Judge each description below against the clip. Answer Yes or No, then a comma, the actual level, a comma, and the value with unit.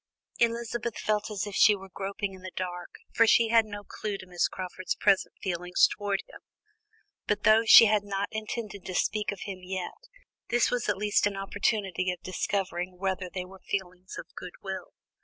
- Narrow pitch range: Yes, narrow, 2.3 semitones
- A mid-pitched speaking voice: No, high, 200 Hz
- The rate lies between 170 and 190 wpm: Yes, average, 185 wpm